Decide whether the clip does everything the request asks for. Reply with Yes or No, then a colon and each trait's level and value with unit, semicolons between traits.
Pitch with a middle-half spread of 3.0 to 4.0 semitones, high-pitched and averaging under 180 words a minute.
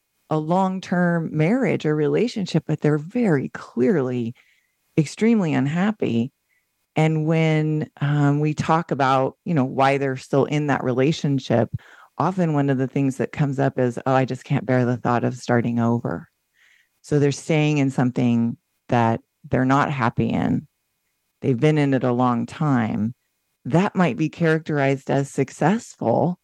No: average, 3.7 semitones; medium, 140 Hz; average, 155 wpm